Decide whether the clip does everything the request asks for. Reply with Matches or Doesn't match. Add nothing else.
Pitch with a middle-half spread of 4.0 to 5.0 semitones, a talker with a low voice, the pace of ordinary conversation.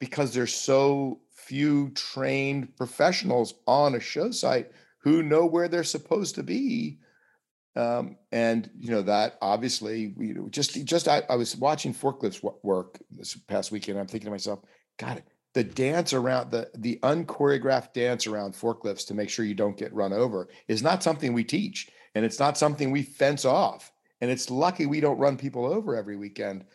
Matches